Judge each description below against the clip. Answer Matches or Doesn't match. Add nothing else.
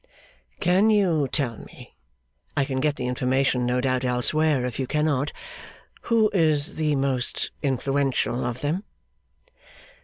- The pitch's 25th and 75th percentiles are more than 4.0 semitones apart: Doesn't match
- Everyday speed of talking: Doesn't match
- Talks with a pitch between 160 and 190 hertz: Doesn't match